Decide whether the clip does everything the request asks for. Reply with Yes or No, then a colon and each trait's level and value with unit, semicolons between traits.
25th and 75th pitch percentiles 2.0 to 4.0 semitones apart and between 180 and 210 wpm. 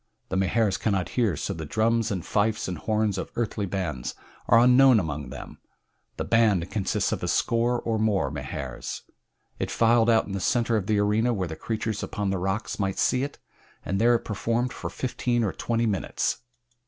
Yes: average, 3.4 semitones; average, 190 wpm